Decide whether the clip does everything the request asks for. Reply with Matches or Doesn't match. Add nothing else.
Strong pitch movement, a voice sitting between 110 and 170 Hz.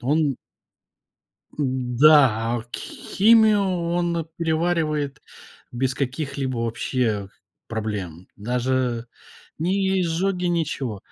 Matches